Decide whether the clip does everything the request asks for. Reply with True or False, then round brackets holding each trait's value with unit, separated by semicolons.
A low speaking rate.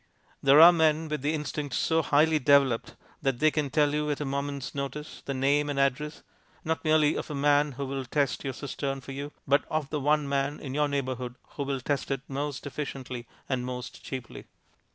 False (205 wpm)